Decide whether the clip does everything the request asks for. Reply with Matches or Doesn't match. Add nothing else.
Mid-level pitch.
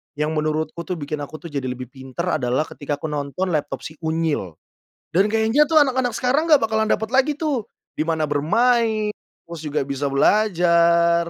Matches